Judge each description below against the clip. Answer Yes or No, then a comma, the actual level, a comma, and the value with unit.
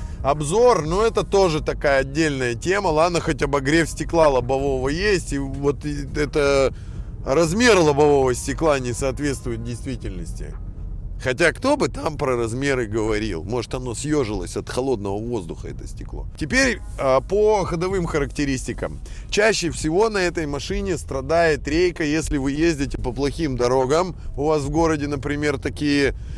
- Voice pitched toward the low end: No, medium, 145 Hz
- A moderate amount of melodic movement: Yes, average, 4.3 semitones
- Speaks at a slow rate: No, average, 135 wpm